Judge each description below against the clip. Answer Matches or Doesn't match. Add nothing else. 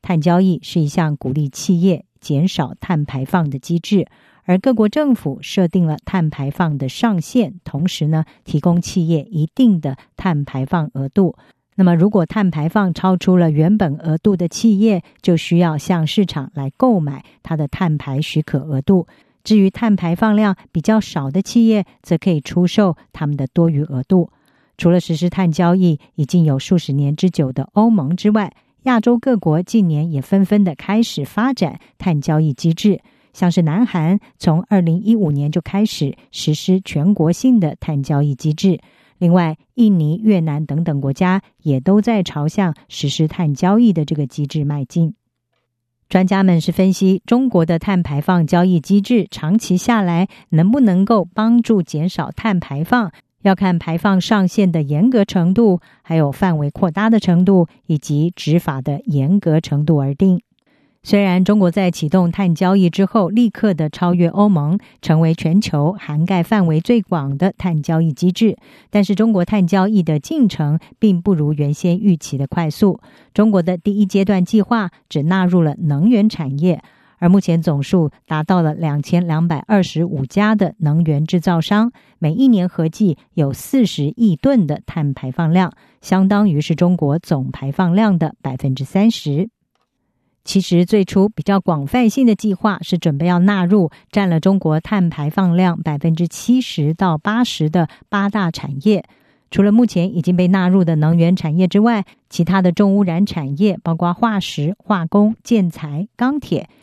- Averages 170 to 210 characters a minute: Doesn't match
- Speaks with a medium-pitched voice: Matches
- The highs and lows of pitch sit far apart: Doesn't match